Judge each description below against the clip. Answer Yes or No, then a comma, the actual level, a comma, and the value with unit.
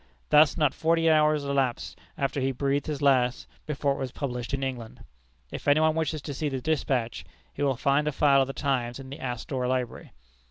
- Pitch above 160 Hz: No, medium, 140 Hz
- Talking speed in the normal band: No, fast, 210 wpm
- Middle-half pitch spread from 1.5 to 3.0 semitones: Yes, narrow, 2.5 semitones